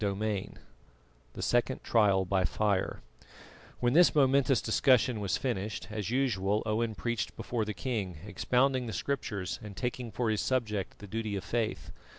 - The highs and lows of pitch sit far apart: No, average, 3.5 semitones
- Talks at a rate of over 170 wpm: No, average, 160 wpm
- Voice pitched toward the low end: Yes, low, 110 Hz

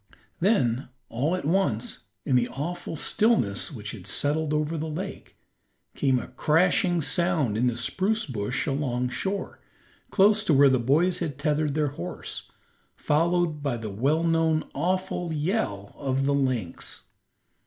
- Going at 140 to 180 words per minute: Yes, average, 145 wpm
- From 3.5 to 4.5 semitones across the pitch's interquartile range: No, wide, 5.4 semitones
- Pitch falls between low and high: Yes, medium, 150 Hz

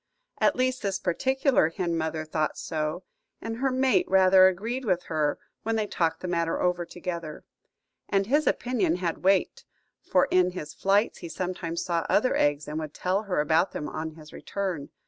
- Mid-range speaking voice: Yes, medium, 180 Hz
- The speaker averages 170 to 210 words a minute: Yes, average, 180 wpm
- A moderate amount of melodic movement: Yes, average, 3.7 semitones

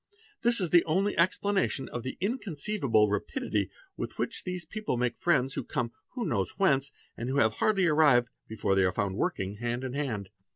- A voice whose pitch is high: No, low, 135 Hz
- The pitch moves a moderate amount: No, wide, 7.8 semitones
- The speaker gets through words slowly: No, average, 195 wpm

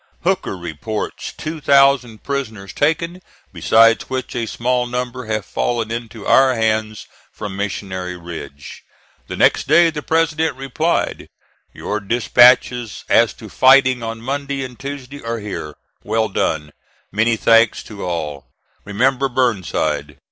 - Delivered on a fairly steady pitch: No, average, 4.5 semitones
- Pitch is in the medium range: No, low, 115 Hz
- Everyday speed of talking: No, slow, 130 wpm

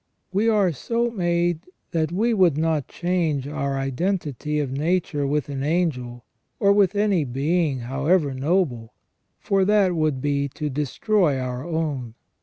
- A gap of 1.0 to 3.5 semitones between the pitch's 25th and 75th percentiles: No, average, 4.9 semitones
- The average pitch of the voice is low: No, medium, 155 Hz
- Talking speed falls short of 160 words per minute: Yes, average, 145 wpm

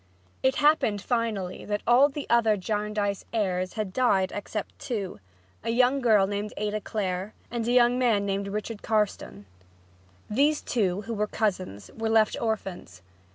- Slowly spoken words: No, average, 155 wpm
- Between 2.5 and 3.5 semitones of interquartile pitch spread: Yes, average, 2.9 semitones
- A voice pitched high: Yes, high, 210 Hz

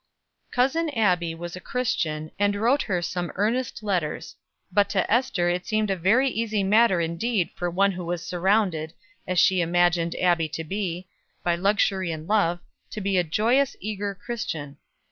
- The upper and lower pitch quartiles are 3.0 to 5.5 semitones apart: Yes, average, 3.7 semitones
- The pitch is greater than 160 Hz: Yes, high, 190 Hz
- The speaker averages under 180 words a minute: Yes, average, 165 wpm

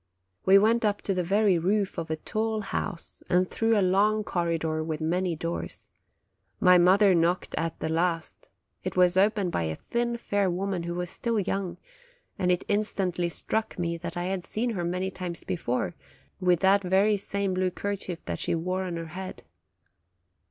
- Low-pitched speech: No, medium, 185 Hz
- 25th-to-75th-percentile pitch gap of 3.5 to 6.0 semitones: No, average, 2.7 semitones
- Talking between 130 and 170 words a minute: No, average, 180 wpm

